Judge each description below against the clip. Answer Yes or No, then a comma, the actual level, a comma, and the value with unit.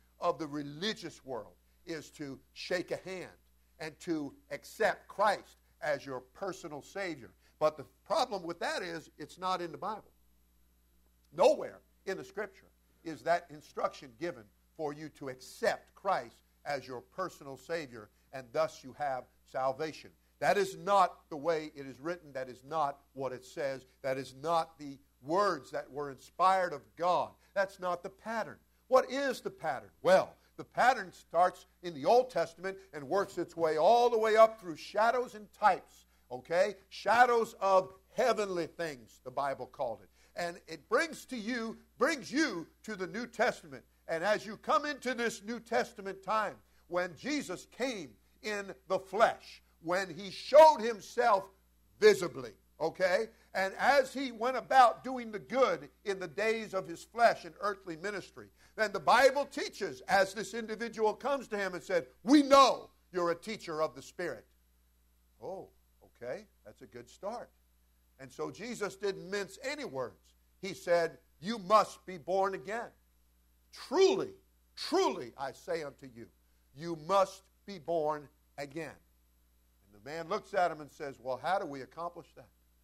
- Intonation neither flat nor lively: No, wide, 7.5 semitones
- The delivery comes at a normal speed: Yes, average, 165 wpm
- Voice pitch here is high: No, medium, 170 Hz